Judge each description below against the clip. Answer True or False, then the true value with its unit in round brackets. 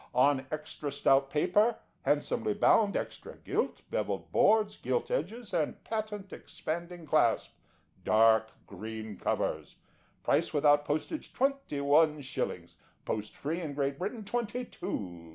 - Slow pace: True (120 wpm)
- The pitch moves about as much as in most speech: False (7.2 semitones)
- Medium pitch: True (155 Hz)